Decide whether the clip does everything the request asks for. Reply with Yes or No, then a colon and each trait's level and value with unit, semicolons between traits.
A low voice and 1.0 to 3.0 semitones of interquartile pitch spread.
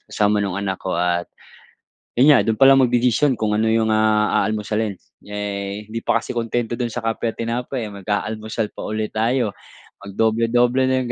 Yes: low, 110 Hz; narrow, 2.6 semitones